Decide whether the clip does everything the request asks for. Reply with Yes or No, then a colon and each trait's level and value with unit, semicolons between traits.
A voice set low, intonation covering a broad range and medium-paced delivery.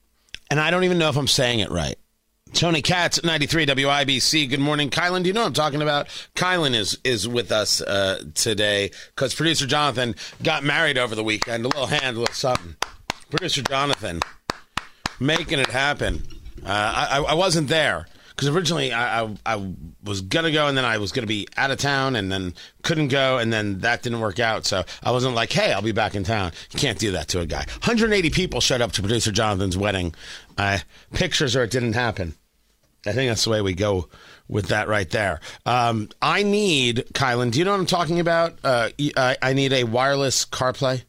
No: low, 125 Hz; wide, 5.9 semitones; fast, 210 wpm